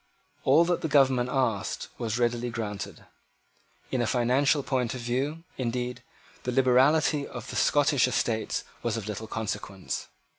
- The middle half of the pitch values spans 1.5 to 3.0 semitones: Yes, average, 2.7 semitones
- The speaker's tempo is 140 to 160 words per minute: Yes, average, 145 wpm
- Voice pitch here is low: Yes, low, 125 Hz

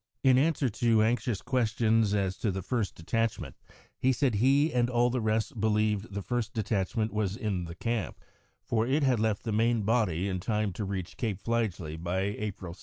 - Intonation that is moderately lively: Yes, average, 3.2 semitones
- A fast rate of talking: No, average, 190 wpm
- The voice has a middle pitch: No, low, 110 Hz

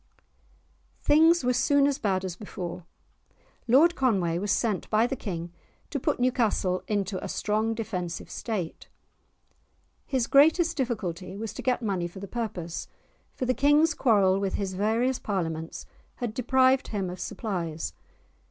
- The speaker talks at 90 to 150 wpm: Yes, average, 145 wpm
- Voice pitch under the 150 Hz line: No, high, 215 Hz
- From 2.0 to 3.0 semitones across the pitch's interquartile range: No, wide, 5.5 semitones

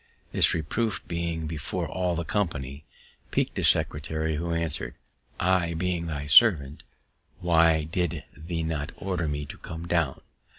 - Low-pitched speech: Yes, very low, 80 Hz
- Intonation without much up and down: Yes, narrow, 2.2 semitones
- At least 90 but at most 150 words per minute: Yes, average, 140 wpm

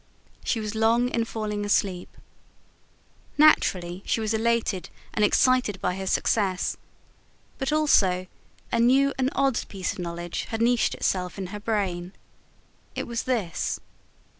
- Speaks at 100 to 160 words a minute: Yes, average, 140 wpm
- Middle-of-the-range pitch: No, high, 215 Hz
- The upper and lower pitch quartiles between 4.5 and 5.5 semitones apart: No, average, 4.1 semitones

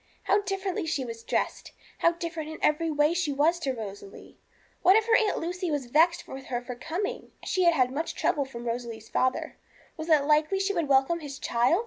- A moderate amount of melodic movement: Yes, average, 4.8 semitones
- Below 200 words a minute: No, fast, 205 wpm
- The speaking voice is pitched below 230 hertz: No, very high, 310 Hz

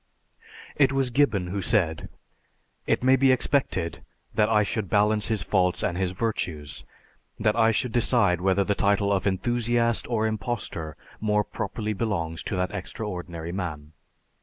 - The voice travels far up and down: No, average, 4.1 semitones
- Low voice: Yes, low, 105 Hz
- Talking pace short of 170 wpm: Yes, average, 150 wpm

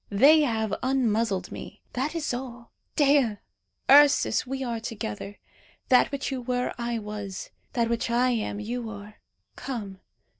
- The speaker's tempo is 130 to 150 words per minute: Yes, average, 145 wpm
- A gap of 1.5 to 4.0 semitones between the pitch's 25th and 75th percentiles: Yes, average, 3.6 semitones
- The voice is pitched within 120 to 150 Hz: No, high, 235 Hz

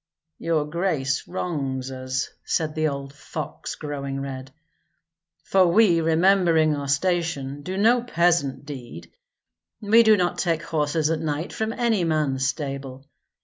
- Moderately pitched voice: Yes, medium, 155 Hz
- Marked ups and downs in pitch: No, average, 4.2 semitones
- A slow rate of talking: Yes, slow, 130 wpm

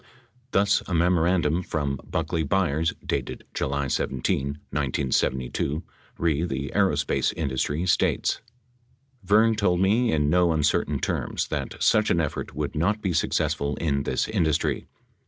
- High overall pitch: No, very low, 80 Hz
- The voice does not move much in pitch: No, average, 4.3 semitones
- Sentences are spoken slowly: Yes, slow, 130 wpm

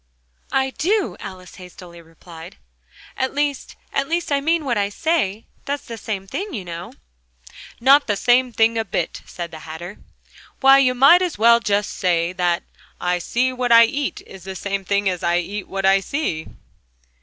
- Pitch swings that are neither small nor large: No, wide, 6.9 semitones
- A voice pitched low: No, high, 210 Hz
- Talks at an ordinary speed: Yes, average, 180 wpm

